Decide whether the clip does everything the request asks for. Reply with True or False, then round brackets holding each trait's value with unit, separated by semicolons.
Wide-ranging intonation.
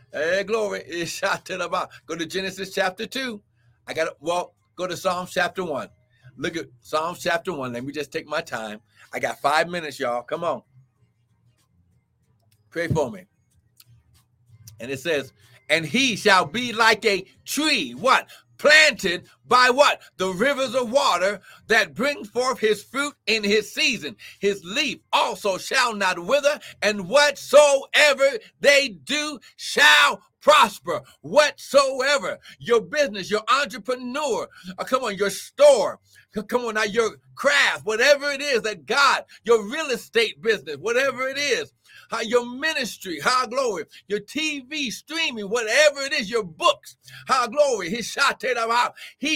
True (9.0 semitones)